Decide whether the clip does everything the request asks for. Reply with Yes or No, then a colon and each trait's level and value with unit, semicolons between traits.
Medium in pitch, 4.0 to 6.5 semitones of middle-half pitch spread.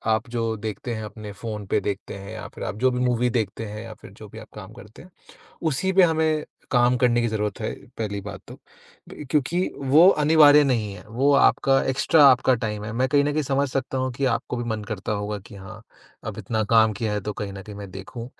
No: low, 115 Hz; average, 4.3 semitones